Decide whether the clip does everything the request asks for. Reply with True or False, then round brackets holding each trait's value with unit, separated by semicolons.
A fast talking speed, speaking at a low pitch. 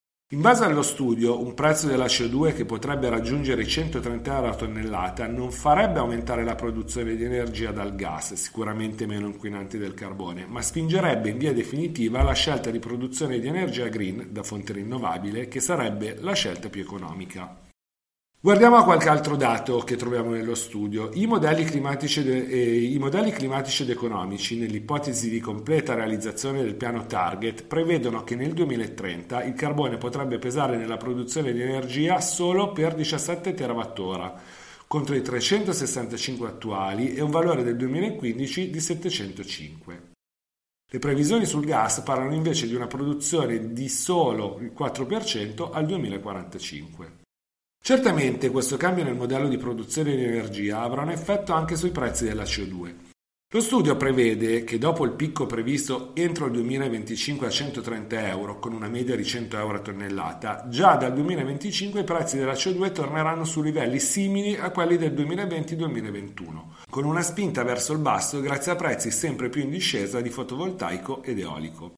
False (155 wpm; 125 Hz)